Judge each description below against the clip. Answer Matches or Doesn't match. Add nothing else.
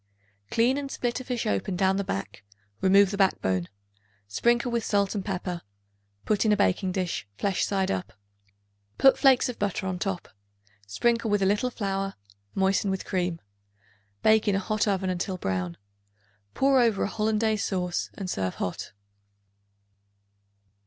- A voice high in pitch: Matches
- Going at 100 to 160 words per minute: Matches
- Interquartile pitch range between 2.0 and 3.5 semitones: Matches